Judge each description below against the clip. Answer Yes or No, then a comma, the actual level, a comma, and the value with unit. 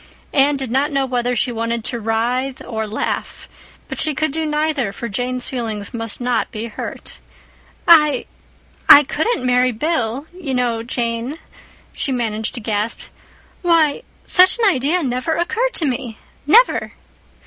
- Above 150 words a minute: No, average, 145 wpm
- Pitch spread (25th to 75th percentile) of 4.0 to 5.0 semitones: Yes, average, 4.5 semitones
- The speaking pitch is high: Yes, very high, 255 Hz